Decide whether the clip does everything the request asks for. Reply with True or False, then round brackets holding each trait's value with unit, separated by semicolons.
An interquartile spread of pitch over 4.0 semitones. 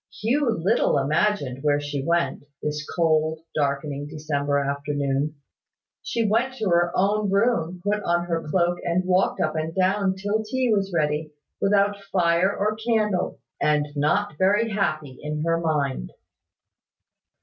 True (5.2 semitones)